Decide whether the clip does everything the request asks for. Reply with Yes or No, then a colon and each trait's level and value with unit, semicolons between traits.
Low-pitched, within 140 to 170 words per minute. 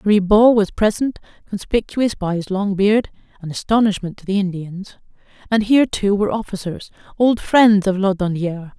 No: high, 200 Hz; average, 150 wpm